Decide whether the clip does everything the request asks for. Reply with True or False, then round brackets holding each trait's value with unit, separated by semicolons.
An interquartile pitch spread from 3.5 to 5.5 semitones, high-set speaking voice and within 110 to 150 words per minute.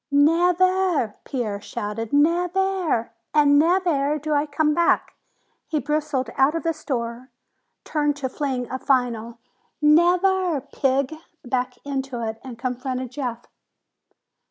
True (4.1 semitones; 285 Hz; 135 wpm)